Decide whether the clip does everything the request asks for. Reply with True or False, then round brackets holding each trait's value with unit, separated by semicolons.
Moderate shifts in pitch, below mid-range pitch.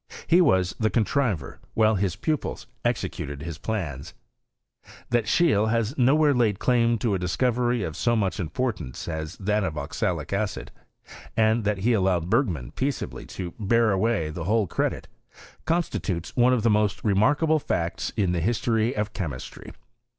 True (4.8 semitones; 105 Hz)